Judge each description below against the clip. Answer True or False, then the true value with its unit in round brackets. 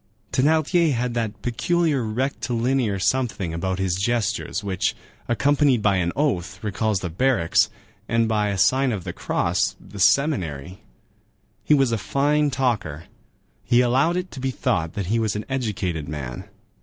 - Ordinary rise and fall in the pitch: False (5.9 semitones)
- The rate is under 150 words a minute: False (155 wpm)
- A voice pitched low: True (115 Hz)